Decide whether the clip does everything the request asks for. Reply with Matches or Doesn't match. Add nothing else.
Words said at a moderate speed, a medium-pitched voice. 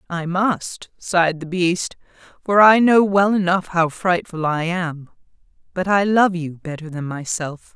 Matches